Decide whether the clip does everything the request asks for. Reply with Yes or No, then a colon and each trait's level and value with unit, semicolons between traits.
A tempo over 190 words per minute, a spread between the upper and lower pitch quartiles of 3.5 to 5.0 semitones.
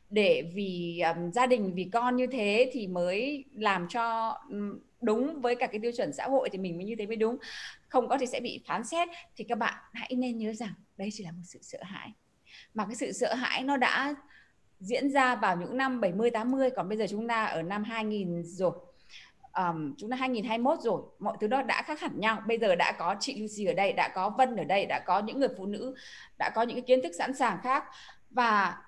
Yes: average, 235 wpm; average, 4.2 semitones